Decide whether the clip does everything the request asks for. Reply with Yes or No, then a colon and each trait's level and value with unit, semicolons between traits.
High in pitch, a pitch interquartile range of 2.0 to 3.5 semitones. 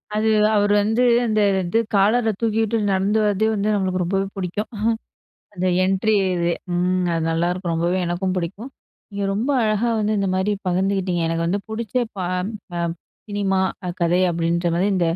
Yes: high, 195 Hz; average, 3.1 semitones